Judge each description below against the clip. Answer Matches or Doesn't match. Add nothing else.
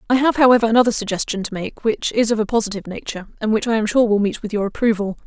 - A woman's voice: Matches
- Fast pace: Matches